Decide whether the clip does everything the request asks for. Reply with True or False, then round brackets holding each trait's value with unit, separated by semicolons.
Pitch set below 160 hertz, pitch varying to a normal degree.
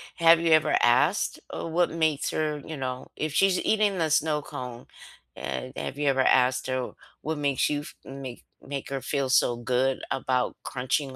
True (140 Hz; 3.5 semitones)